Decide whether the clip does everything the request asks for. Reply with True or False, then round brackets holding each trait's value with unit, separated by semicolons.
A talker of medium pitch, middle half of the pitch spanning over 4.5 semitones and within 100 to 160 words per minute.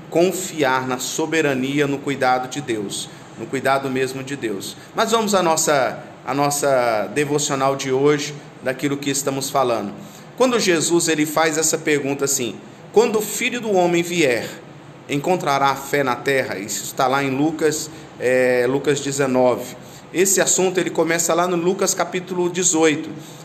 False (150 Hz; 3.6 semitones; 155 wpm)